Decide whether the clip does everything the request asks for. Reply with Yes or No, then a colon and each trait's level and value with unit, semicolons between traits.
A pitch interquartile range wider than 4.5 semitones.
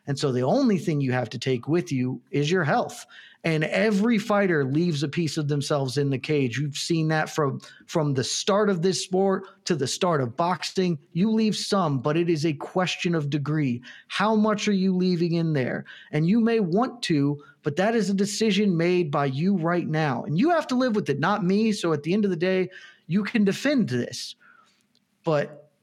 Yes: average, 5.2 semitones